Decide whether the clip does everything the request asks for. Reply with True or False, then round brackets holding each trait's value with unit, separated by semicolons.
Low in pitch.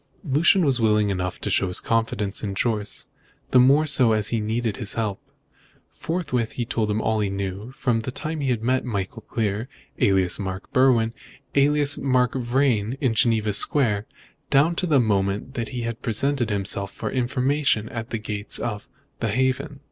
True (115 Hz)